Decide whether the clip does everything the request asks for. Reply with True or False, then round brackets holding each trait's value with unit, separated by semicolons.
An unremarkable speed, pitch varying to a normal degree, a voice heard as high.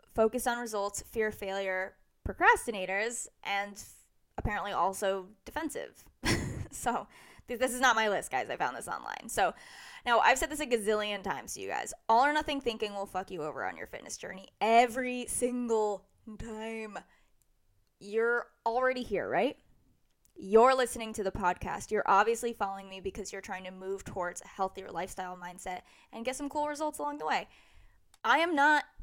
True (175 wpm; 4.2 semitones; 215 Hz)